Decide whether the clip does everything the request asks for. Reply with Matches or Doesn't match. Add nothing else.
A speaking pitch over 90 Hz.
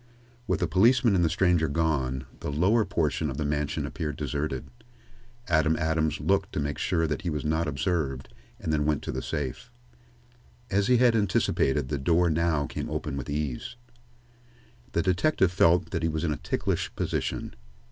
Doesn't match